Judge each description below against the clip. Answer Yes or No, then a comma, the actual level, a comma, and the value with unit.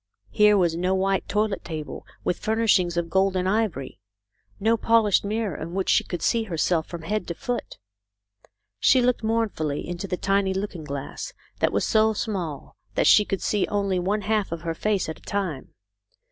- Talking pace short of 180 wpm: No, average, 185 wpm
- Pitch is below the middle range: No, high, 195 Hz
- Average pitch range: Yes, average, 3.8 semitones